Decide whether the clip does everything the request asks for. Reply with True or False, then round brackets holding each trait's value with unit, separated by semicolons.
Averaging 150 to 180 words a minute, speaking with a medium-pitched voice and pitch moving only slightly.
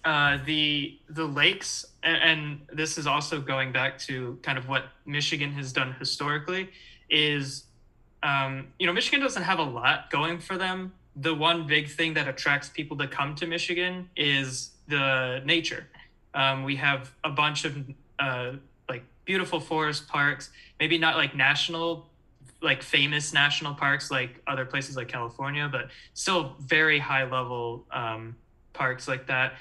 False (160 wpm; 145 Hz; 3.3 semitones)